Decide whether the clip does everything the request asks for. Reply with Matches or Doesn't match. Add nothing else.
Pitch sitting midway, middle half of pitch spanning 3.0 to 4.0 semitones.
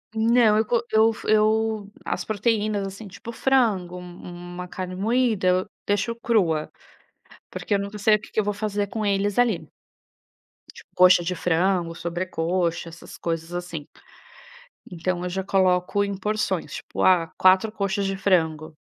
Doesn't match